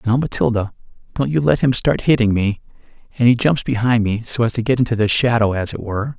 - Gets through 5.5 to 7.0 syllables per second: Yes, 6.1 syllables/s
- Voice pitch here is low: Yes, low, 120 Hz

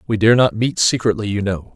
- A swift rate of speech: Yes, fast, 240 wpm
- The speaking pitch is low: Yes, low, 105 Hz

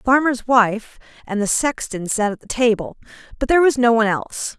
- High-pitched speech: Yes, high, 230 Hz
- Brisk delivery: Yes, fast, 210 wpm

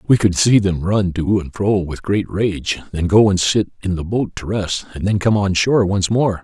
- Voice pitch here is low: Yes, very low, 95 Hz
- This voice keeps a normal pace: No, fast, 250 wpm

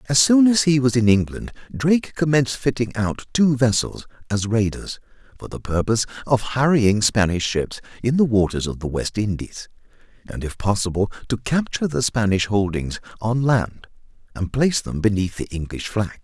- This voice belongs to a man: Yes, male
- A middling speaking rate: Yes, average, 170 wpm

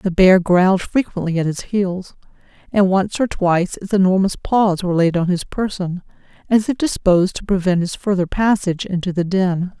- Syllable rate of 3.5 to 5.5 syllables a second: Yes, 5.2 syllables/s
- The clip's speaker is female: Yes, female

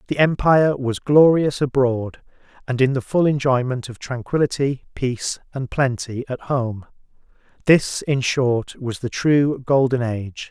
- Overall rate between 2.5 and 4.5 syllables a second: Yes, 4.3 syllables/s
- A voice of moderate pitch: No, low, 130 Hz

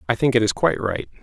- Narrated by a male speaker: Yes, male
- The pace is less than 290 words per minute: No, fast, 295 wpm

